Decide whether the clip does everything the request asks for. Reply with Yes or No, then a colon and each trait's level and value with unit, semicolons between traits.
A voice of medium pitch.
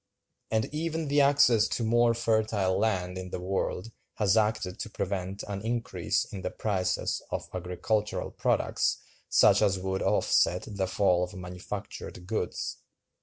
No: low, 100 Hz